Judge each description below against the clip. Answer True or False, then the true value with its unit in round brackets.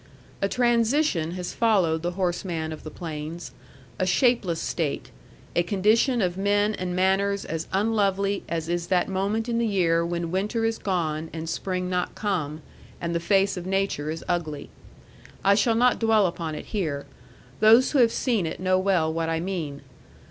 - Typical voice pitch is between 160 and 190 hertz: True (185 Hz)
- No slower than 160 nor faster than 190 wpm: True (175 wpm)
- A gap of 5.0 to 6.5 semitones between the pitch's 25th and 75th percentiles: False (3.7 semitones)